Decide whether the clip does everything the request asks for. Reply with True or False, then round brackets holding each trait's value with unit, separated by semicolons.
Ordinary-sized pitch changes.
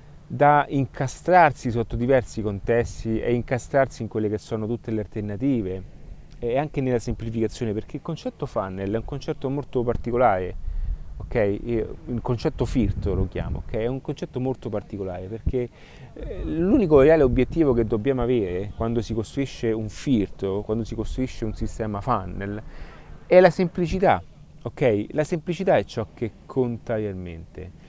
True (4.0 semitones)